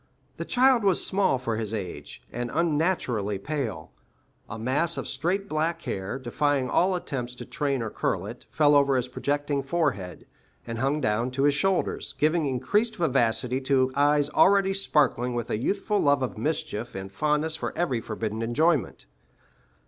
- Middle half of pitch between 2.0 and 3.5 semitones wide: No, average, 5.2 semitones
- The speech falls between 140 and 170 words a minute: Yes, average, 165 wpm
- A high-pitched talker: No, medium, 140 Hz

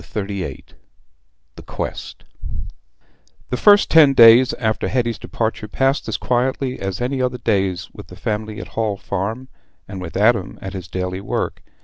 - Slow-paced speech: No, average, 160 wpm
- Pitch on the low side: Yes, low, 110 Hz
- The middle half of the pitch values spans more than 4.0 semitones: Yes, average, 4.4 semitones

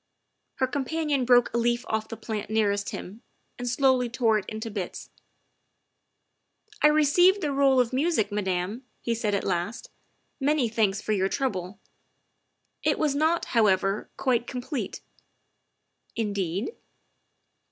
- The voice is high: Yes, high, 235 Hz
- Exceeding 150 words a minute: No, average, 140 wpm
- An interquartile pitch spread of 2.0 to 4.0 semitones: No, average, 4.7 semitones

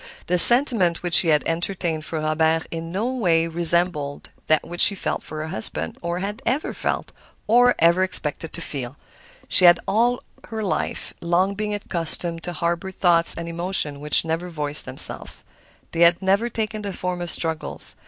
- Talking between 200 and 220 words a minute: No, average, 175 wpm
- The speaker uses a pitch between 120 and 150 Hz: No, medium, 170 Hz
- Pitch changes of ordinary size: Yes, average, 3.0 semitones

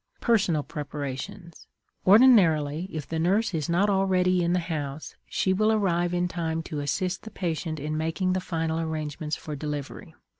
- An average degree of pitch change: Yes, average, 3.3 semitones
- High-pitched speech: No, medium, 165 Hz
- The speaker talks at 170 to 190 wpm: No, average, 160 wpm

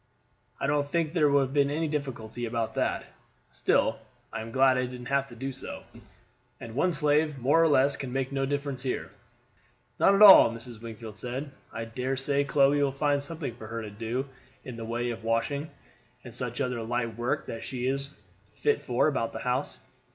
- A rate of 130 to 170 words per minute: No, average, 200 wpm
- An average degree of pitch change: Yes, average, 3.4 semitones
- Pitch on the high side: No, low, 130 Hz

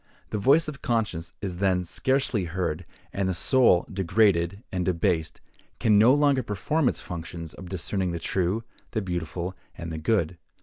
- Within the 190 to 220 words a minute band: No, average, 165 wpm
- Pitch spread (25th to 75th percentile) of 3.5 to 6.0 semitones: Yes, average, 4.4 semitones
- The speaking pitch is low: Yes, very low, 95 Hz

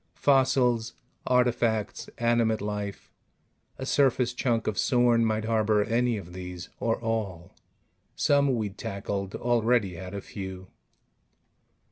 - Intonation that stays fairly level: No, average, 3.3 semitones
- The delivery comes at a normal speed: No, slow, 115 wpm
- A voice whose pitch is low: Yes, low, 110 Hz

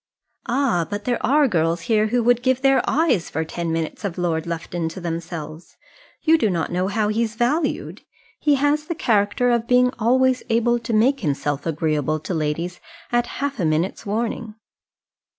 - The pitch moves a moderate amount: No, wide, 6.9 semitones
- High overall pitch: Yes, high, 215 Hz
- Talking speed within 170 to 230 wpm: Yes, average, 175 wpm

